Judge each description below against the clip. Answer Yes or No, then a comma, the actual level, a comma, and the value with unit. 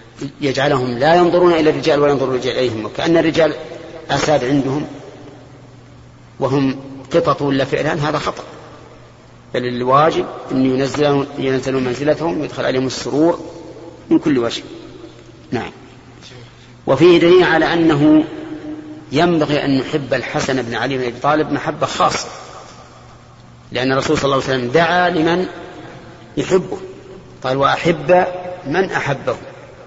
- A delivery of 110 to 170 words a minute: Yes, average, 120 wpm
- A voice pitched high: No, medium, 145 Hz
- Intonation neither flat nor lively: Yes, average, 3.9 semitones